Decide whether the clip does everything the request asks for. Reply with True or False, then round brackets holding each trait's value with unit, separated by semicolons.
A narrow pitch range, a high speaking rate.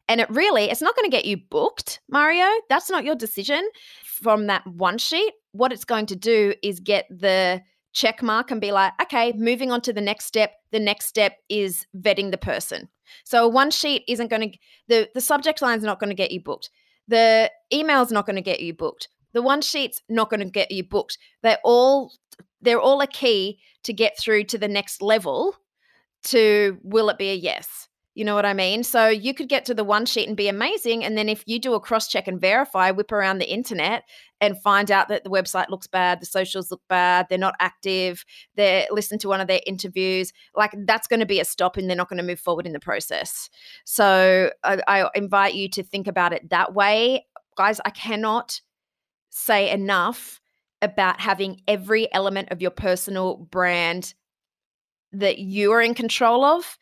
False (3.7 semitones; 210 wpm)